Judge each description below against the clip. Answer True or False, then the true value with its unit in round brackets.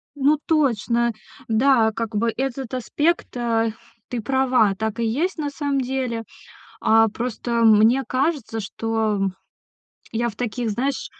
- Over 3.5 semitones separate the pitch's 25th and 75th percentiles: False (3.1 semitones)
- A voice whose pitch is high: True (235 Hz)